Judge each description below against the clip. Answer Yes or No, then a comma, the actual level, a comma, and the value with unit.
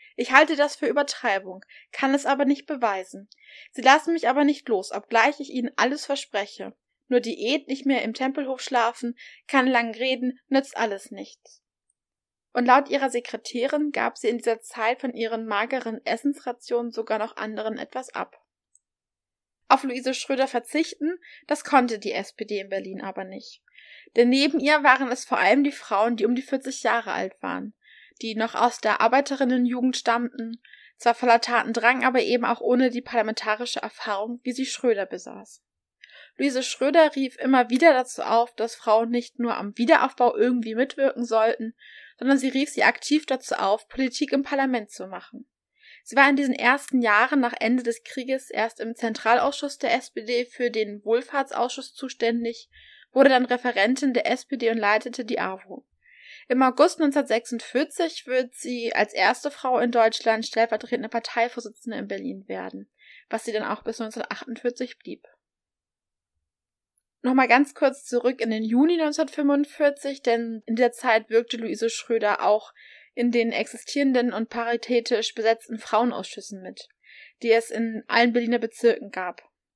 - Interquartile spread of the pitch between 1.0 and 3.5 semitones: Yes, average, 2.9 semitones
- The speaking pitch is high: Yes, high, 245 Hz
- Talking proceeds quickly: No, average, 155 wpm